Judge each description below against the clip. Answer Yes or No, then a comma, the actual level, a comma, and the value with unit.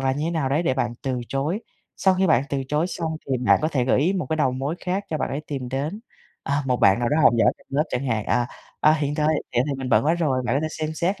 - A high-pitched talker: No, medium, 145 Hz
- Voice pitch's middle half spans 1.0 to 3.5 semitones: Yes, average, 3.2 semitones